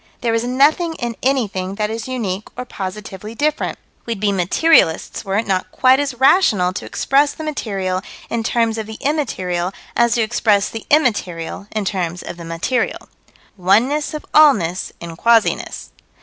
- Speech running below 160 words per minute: No, average, 165 wpm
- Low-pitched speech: No, high, 220 Hz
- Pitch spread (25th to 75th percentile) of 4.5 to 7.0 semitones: Yes, wide, 5.4 semitones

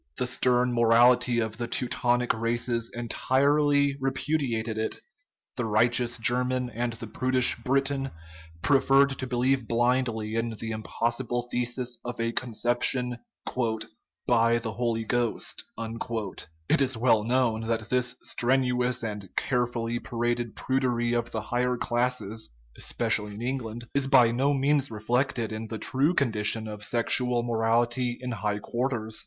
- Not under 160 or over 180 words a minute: No, slow, 135 wpm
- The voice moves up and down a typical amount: No, narrow, 1.9 semitones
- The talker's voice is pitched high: No, low, 120 Hz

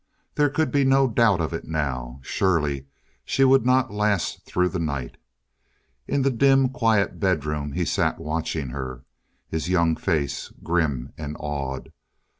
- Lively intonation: Yes, wide, 8.4 semitones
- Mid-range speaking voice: No, very low, 80 Hz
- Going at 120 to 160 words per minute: Yes, average, 150 wpm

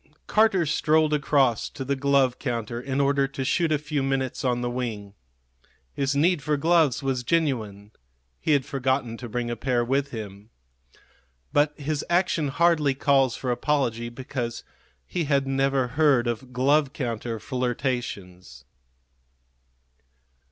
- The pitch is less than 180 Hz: Yes, low, 135 Hz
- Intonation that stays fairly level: No, average, 3.2 semitones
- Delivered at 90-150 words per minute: Yes, average, 140 wpm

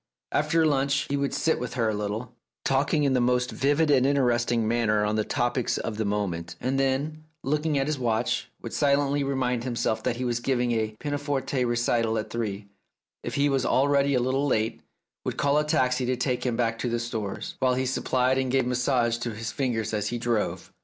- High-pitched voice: No, low, 125 Hz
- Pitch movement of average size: Yes, average, 3.2 semitones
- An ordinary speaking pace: No, fast, 210 wpm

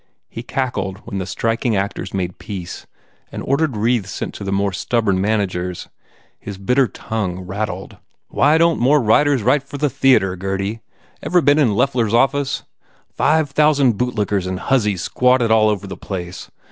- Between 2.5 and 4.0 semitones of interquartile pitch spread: No, wide, 5.6 semitones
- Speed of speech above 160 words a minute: Yes, average, 175 wpm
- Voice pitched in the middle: No, low, 110 Hz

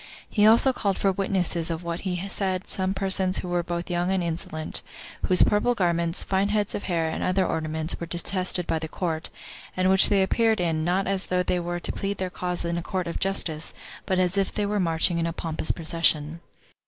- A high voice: No, medium, 180 Hz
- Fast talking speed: Yes, fast, 215 wpm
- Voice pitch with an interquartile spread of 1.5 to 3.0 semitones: Yes, narrow, 2.4 semitones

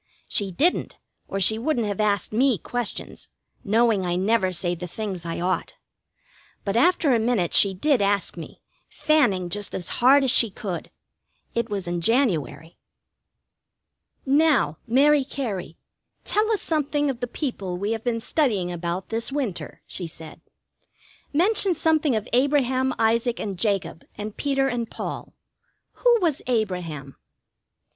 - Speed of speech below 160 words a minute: Yes, average, 145 wpm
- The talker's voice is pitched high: Yes, high, 225 Hz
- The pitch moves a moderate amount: No, wide, 6.6 semitones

